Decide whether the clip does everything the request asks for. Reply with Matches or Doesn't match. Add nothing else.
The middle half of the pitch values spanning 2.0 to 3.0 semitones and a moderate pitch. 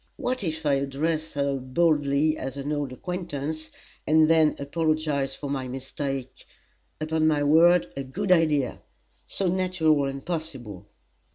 Matches